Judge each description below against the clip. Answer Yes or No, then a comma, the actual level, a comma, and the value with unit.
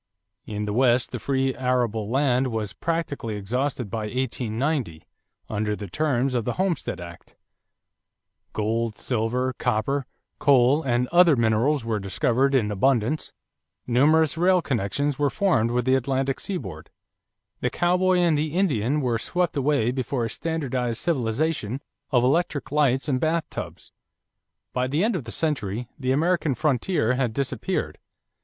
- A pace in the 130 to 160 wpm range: Yes, average, 140 wpm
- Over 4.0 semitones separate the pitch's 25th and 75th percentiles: Yes, average, 4.6 semitones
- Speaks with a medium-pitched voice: No, low, 130 Hz